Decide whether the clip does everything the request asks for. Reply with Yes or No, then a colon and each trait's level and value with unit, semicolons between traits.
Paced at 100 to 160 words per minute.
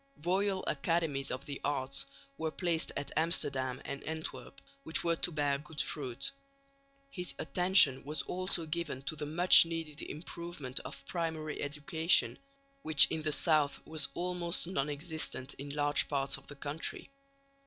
Yes: average, 150 wpm